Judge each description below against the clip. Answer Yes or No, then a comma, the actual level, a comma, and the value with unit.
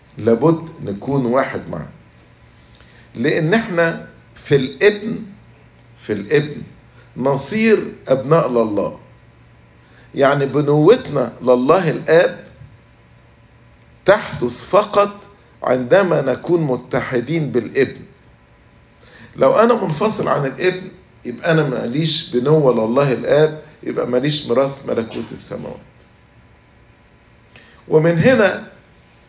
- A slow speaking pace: Yes, slow, 85 wpm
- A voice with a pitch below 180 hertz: Yes, medium, 140 Hz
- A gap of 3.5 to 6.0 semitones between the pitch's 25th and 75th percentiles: Yes, wide, 5.6 semitones